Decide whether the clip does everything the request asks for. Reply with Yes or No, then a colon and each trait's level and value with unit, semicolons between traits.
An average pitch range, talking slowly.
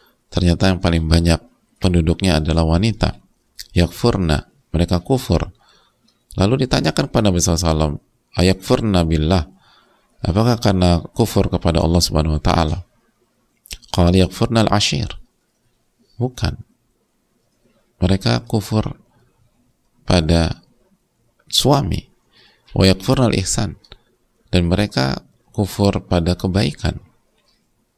Yes: average, 3.2 semitones; slow, 85 wpm